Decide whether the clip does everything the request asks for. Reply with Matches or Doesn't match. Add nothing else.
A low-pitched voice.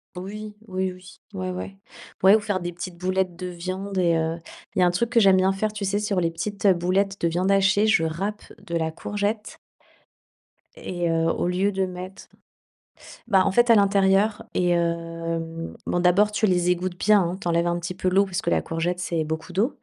Doesn't match